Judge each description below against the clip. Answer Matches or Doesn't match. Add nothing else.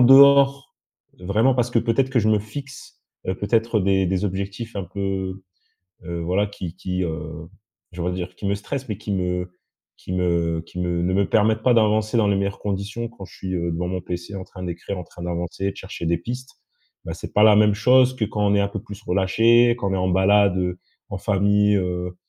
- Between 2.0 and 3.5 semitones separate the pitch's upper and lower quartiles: Matches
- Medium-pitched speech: Doesn't match